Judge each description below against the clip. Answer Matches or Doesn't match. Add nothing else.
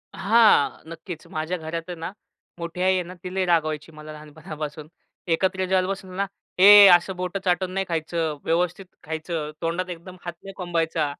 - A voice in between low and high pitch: Matches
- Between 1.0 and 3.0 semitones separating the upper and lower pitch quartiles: Matches